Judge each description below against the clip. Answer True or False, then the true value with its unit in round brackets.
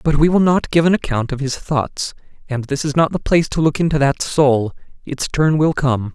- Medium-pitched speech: True (145 Hz)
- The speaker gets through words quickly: True (235 wpm)